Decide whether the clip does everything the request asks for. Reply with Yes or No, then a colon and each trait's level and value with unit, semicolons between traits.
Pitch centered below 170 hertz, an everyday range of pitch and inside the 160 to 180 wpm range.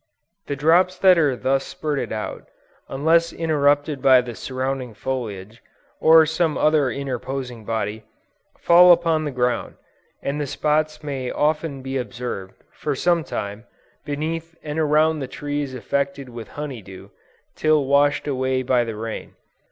No: medium, 140 Hz; average, 3.7 semitones; average, 145 wpm